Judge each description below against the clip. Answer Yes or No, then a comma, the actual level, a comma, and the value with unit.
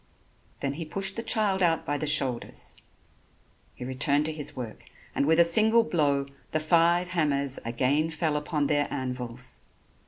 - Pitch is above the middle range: No, medium, 150 Hz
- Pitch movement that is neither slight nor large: Yes, average, 3.6 semitones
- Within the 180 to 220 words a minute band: No, average, 160 wpm